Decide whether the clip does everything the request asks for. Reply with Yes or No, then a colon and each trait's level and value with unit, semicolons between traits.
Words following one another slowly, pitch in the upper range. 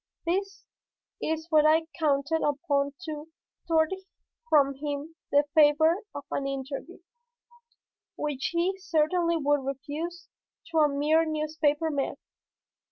Yes: slow, 115 wpm; very high, 305 Hz